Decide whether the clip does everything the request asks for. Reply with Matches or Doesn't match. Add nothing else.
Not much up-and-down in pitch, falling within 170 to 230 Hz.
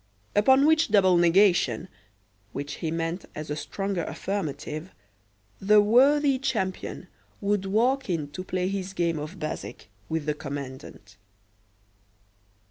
Doesn't match